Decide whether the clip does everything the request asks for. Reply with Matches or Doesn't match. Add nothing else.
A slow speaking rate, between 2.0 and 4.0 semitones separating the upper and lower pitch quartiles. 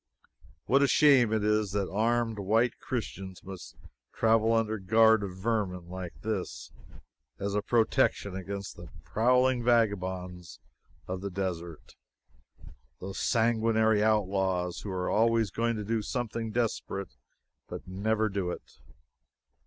Matches